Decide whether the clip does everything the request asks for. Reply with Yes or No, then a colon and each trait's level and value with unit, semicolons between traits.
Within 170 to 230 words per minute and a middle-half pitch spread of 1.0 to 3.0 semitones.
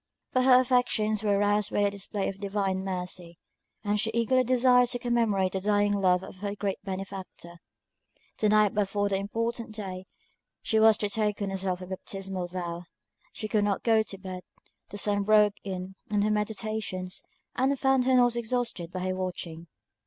Yes: average, 180 wpm; average, 2.7 semitones